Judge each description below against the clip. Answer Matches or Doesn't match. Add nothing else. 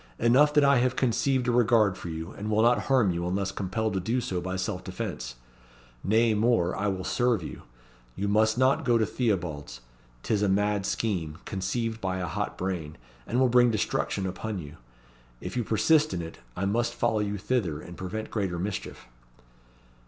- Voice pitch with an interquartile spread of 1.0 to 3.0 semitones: Doesn't match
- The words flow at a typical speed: Matches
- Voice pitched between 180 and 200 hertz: Doesn't match